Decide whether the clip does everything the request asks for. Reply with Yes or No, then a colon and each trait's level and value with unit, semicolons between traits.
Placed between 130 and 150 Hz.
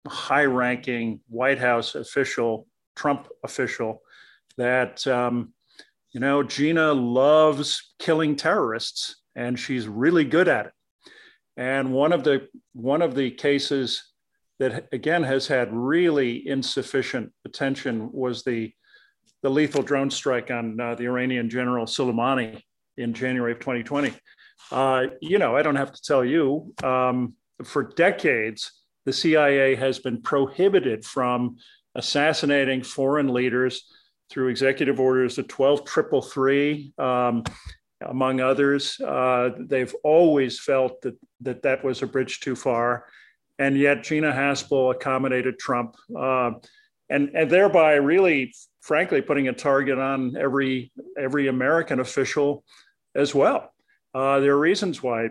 Yes: low, 135 Hz